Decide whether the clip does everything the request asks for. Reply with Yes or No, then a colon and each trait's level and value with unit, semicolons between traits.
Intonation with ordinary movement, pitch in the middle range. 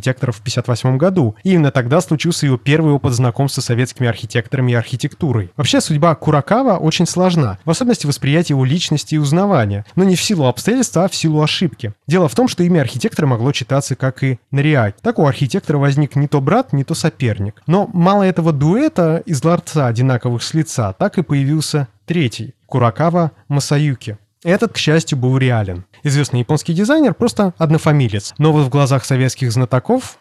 Yes: average, 4.9 semitones; medium, 145 Hz